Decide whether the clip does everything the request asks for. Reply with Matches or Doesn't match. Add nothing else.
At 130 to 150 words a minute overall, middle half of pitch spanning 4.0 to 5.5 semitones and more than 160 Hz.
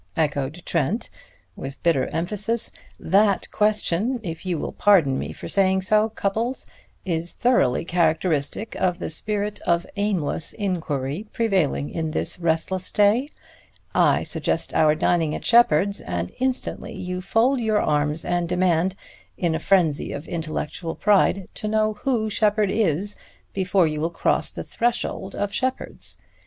Matches